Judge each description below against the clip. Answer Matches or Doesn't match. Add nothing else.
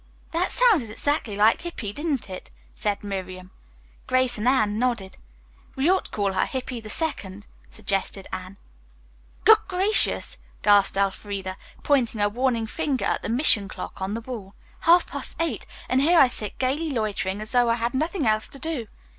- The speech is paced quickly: Doesn't match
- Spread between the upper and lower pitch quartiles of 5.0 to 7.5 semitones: Matches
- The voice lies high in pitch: Matches